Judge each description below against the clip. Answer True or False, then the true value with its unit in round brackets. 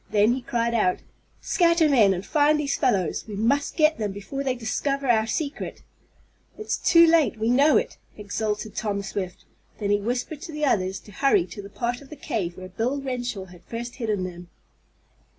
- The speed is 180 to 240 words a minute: True (190 wpm)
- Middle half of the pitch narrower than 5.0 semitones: False (5.6 semitones)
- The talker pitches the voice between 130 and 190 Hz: False (235 Hz)